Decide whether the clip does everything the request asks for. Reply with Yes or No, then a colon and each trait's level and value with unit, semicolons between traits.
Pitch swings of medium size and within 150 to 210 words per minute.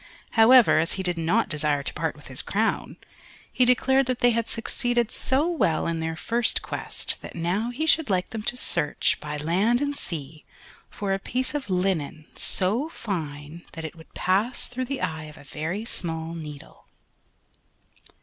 No: wide, 7.1 semitones; average, 180 wpm